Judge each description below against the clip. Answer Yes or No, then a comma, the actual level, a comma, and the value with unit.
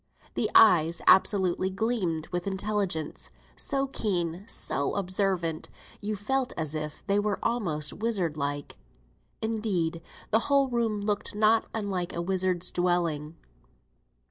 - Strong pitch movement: No, average, 4.2 semitones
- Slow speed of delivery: Yes, slow, 120 wpm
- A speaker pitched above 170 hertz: Yes, high, 190 Hz